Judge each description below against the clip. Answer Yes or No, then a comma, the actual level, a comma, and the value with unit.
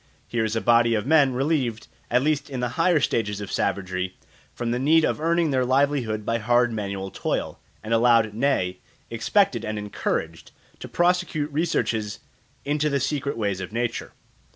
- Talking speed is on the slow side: No, average, 170 wpm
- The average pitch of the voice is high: No, low, 120 Hz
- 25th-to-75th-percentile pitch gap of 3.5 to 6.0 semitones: Yes, average, 5.1 semitones